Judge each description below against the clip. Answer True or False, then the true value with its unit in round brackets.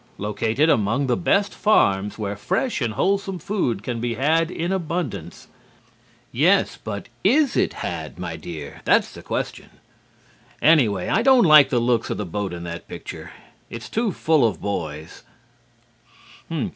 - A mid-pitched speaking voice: False (120 Hz)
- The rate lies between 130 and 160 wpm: True (150 wpm)